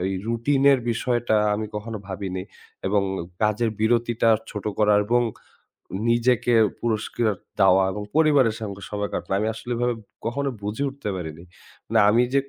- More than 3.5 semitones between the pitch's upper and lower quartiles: No, average, 2.8 semitones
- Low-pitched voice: Yes, low, 115 Hz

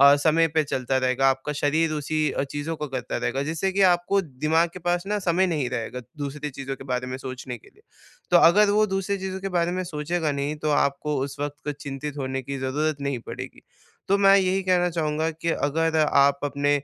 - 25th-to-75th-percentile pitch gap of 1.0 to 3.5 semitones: No, average, 3.9 semitones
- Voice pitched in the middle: Yes, medium, 150 Hz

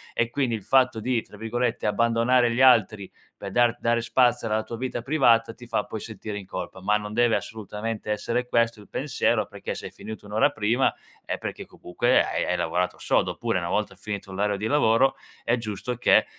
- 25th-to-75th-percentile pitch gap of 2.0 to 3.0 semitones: Yes, narrow, 2.5 semitones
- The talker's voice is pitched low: Yes, low, 115 Hz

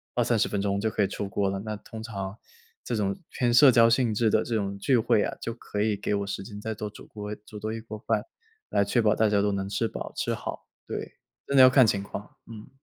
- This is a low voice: Yes, low, 105 Hz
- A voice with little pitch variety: Yes, narrow, 2.1 semitones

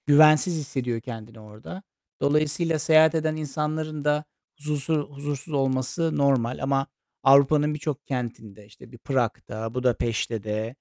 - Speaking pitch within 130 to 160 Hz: Yes, medium, 140 Hz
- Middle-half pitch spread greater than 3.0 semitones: Yes, average, 4.3 semitones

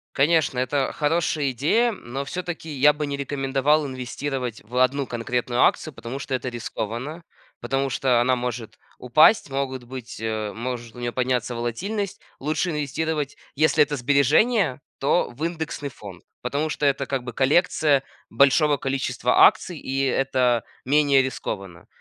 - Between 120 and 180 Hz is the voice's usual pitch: Yes, low, 135 Hz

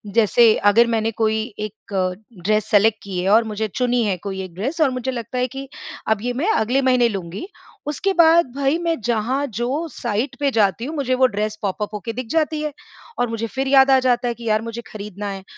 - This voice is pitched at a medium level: No, high, 235 Hz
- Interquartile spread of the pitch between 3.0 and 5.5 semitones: Yes, average, 4.0 semitones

